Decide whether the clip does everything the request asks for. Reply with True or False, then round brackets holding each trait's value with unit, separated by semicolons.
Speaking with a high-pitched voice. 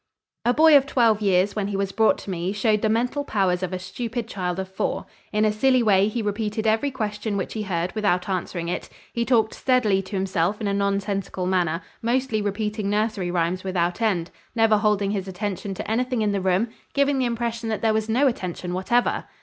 True (210 Hz)